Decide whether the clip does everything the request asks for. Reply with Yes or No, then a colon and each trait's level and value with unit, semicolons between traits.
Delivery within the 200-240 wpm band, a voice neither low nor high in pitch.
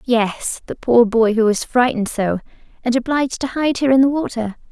No: fast, 205 wpm; high, 240 Hz